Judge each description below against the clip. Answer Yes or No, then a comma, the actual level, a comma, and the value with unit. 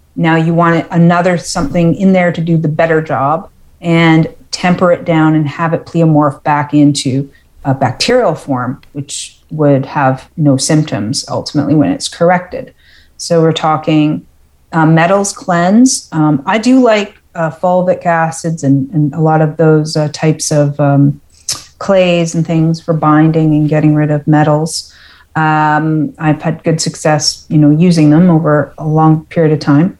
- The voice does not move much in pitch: Yes, narrow, 2.1 semitones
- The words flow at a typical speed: Yes, average, 165 wpm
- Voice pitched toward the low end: No, medium, 155 Hz